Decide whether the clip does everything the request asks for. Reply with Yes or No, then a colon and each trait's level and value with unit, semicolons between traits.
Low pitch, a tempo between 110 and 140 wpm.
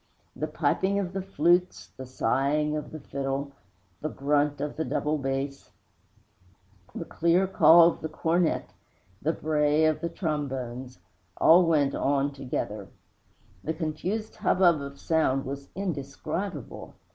No: medium, 150 Hz; slow, 135 wpm